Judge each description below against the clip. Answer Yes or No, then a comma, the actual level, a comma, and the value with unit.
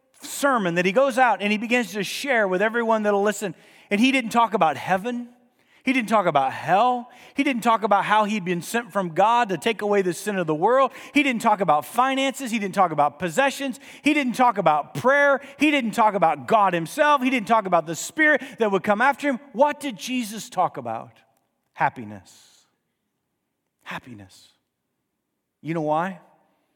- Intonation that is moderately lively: No, wide, 5.9 semitones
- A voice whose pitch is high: Yes, high, 225 Hz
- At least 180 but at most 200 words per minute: Yes, average, 190 wpm